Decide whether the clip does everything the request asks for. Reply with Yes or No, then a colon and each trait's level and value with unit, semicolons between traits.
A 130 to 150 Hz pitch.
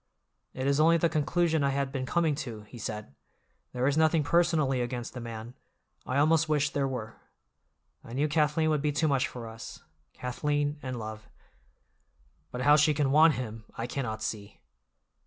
Yes: medium, 140 Hz